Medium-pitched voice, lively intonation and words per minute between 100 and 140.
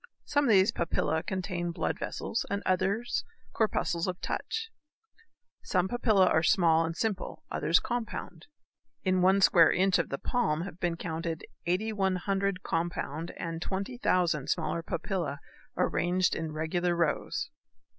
No: medium, 180 Hz; average, 3.0 semitones; slow, 135 wpm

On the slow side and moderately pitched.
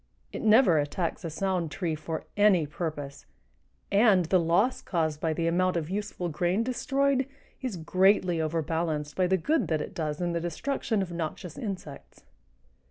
No: average, 165 wpm; medium, 175 Hz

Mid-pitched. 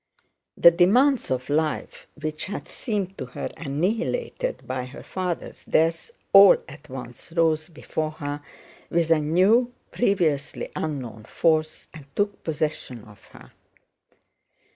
Yes: medium, 160 Hz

